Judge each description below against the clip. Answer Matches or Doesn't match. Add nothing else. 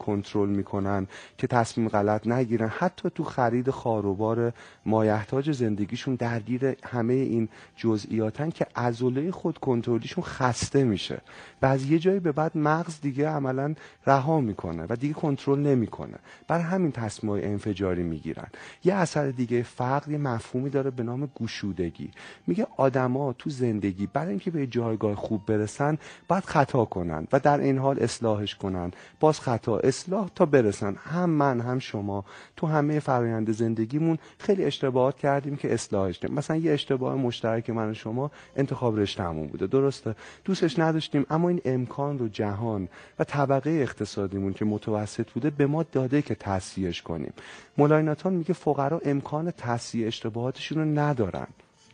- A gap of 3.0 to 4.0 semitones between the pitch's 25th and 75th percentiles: Doesn't match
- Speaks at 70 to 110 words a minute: Doesn't match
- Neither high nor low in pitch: Doesn't match